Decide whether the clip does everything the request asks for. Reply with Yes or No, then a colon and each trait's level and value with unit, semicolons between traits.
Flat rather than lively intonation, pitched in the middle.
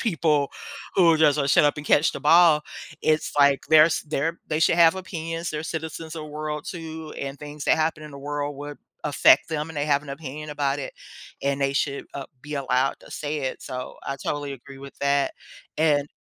Yes: narrow, 2.1 semitones; medium, 150 Hz